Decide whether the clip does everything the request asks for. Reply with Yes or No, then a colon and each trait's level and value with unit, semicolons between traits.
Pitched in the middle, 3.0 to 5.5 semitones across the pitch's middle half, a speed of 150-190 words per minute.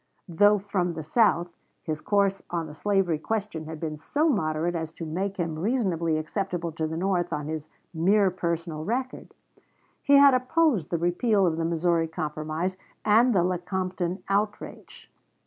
Yes: medium, 175 Hz; average, 4.0 semitones; average, 160 wpm